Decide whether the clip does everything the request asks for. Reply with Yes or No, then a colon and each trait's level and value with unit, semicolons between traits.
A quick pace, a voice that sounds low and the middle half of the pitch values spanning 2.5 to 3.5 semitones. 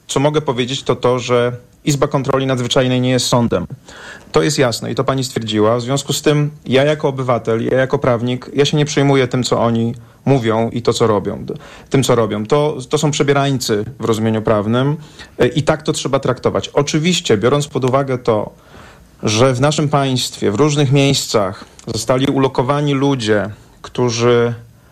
Yes: fast, 175 wpm; low, 130 Hz; average, 3.1 semitones